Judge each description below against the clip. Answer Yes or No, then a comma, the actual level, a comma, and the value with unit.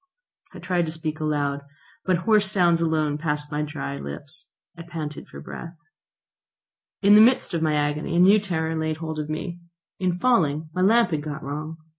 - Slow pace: No, average, 185 wpm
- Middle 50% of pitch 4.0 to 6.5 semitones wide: No, average, 3.0 semitones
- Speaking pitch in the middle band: Yes, medium, 160 Hz